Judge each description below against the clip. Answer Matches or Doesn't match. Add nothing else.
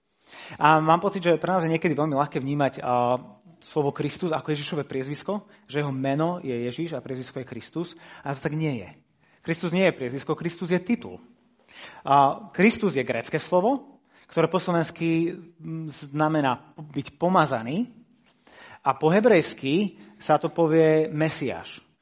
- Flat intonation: Doesn't match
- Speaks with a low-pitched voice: Doesn't match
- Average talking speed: Matches